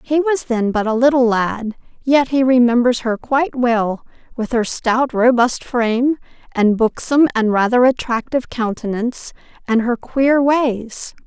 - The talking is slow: No, average, 150 wpm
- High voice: Yes, high, 245 Hz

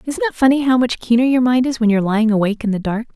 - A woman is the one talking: Yes, female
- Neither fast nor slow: No, fast, 325 wpm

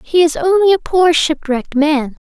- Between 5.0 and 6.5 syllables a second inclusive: No, 4.8 syllables/s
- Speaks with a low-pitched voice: No, very high, 320 Hz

